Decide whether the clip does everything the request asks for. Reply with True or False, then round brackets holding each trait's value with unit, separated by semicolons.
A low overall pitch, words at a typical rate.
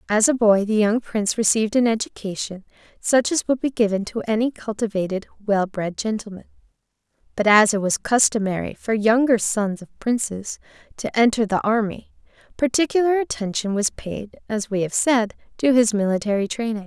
False (220 Hz; 165 wpm)